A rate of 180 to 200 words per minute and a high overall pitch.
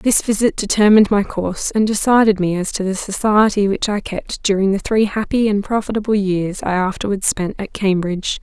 Yes: average, 190 wpm; high, 200 Hz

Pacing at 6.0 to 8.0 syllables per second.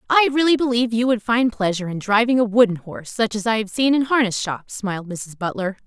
Yes: 6.1 syllables/s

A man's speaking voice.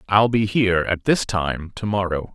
Yes: male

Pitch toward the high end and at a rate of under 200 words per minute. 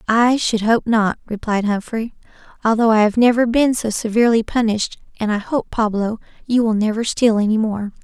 Yes: high, 225 Hz; average, 180 wpm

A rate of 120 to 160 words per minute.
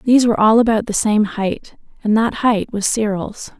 No: average, 200 wpm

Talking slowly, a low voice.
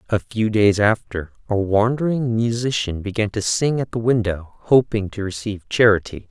No: average, 160 wpm; low, 110 Hz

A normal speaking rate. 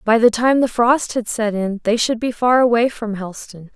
No: fast, 240 wpm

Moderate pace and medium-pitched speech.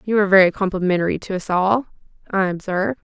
No: average, 175 wpm; high, 195 Hz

